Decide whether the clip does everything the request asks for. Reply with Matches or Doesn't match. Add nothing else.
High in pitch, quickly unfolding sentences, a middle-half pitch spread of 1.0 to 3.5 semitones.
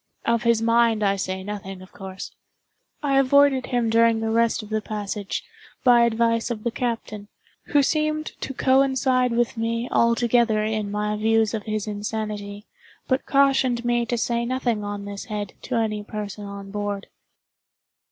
Doesn't match